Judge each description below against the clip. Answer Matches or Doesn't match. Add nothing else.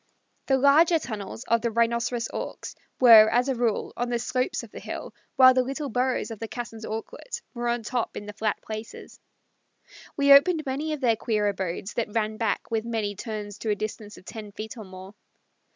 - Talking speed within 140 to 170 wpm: Doesn't match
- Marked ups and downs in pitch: Doesn't match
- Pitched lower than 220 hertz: Doesn't match